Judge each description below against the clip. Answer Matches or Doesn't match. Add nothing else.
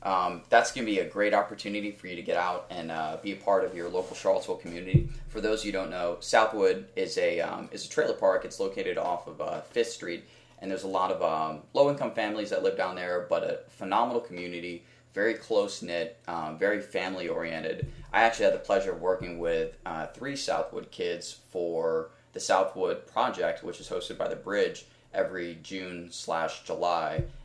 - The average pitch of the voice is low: Matches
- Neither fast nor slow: Matches